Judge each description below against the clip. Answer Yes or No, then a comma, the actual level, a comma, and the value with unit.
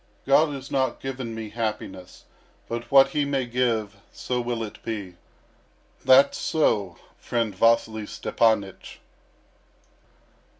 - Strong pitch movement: No, average, 3.6 semitones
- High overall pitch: No, low, 115 Hz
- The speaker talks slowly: Yes, slow, 115 wpm